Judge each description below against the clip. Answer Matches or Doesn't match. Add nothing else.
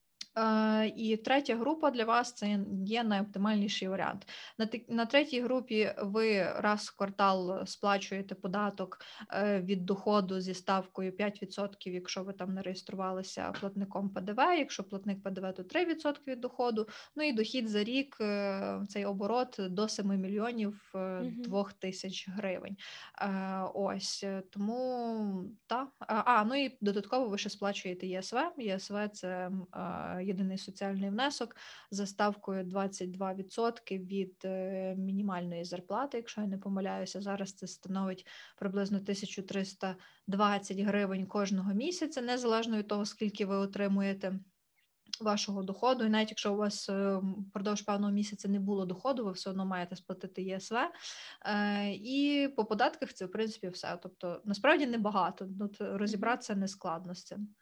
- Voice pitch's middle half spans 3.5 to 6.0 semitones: Doesn't match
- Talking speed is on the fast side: Doesn't match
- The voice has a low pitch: Doesn't match